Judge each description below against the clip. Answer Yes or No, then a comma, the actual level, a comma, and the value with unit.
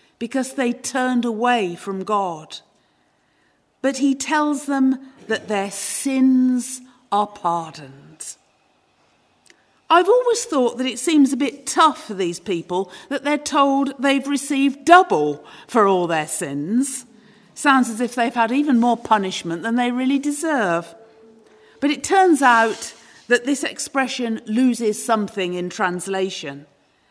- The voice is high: Yes, high, 245 Hz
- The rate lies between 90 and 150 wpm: Yes, slow, 135 wpm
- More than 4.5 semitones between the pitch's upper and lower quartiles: Yes, wide, 5.4 semitones